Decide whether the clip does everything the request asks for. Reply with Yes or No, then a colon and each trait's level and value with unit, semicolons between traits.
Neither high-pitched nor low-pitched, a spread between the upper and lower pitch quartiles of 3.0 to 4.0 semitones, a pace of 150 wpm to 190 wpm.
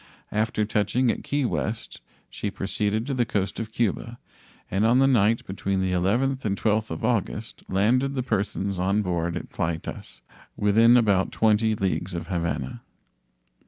No: low, 105 Hz; average, 3.3 semitones; average, 160 wpm